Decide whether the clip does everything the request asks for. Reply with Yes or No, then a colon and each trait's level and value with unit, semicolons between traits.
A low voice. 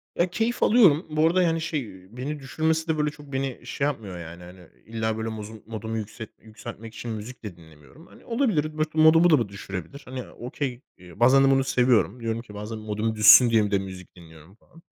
Yes: low, 115 Hz